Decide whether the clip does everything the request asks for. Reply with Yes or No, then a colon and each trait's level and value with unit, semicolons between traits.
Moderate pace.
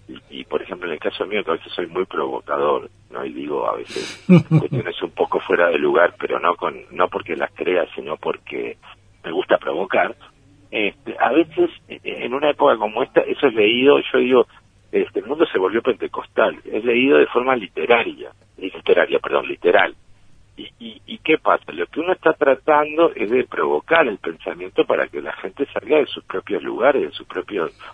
No: fast, 195 wpm